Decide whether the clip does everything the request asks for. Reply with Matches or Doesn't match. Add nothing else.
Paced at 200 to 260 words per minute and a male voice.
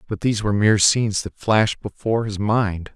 Matches